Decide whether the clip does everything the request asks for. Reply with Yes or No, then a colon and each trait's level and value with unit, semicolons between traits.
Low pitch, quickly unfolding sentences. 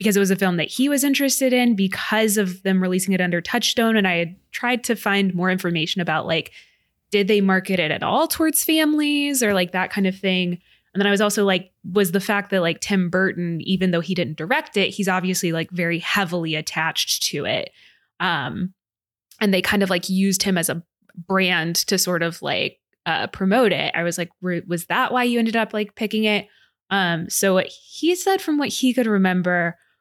No: high, 190 Hz; fast, 215 wpm